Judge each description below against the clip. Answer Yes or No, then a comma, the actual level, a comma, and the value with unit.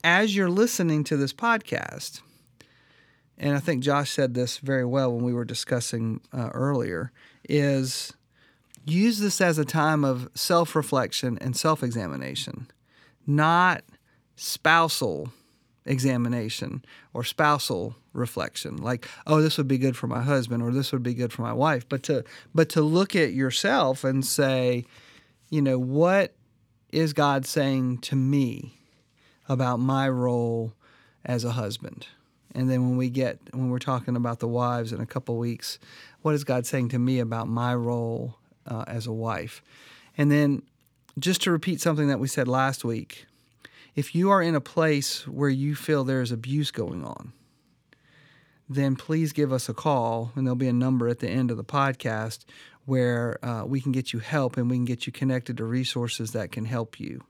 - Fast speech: No, average, 175 wpm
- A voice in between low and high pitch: No, low, 130 Hz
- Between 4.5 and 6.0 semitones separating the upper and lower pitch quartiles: No, average, 3.3 semitones